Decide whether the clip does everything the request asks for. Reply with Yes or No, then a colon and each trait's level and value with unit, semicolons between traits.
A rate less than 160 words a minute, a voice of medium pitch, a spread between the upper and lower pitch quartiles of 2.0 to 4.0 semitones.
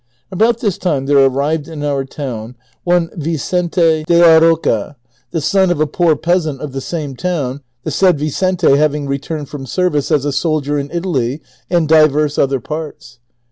No: average, 175 wpm; medium, 155 Hz; average, 3.4 semitones